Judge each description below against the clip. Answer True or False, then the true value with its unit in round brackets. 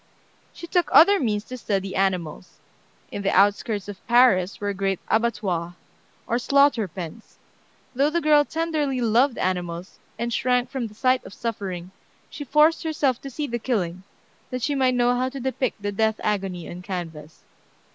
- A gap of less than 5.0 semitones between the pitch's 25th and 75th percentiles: False (5.5 semitones)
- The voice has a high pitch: True (230 Hz)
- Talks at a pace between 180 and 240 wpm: False (165 wpm)